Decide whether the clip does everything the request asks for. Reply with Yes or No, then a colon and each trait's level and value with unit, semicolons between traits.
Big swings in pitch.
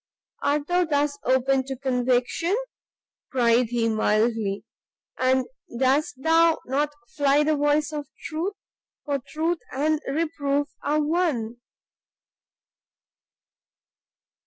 No: average, 3.4 semitones